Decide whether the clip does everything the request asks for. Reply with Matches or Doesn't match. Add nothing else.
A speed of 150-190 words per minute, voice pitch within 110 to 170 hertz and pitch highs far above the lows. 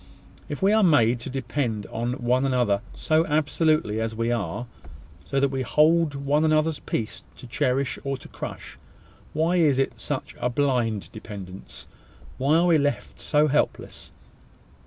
Doesn't match